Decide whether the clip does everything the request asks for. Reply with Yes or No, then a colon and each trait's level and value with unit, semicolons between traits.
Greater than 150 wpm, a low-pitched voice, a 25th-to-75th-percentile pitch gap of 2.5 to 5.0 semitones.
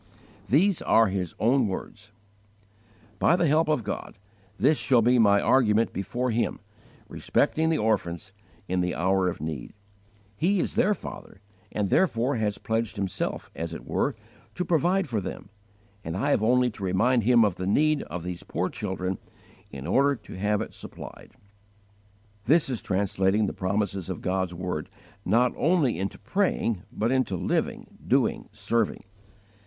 No: average, 160 wpm; low, 110 Hz; wide, 5.6 semitones